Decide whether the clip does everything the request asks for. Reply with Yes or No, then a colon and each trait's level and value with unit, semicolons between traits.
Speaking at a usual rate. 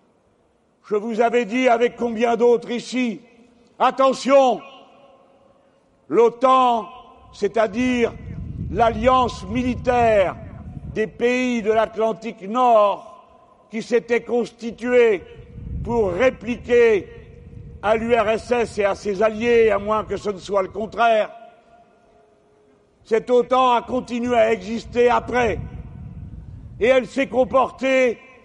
No: slow, 100 wpm